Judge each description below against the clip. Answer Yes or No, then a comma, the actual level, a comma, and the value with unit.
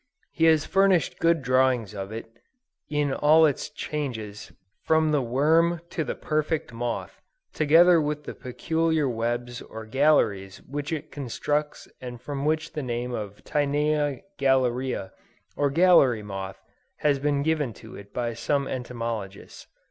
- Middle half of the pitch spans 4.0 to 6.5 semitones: Yes, average, 4.4 semitones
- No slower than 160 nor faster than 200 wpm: No, average, 140 wpm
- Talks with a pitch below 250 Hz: Yes, medium, 140 Hz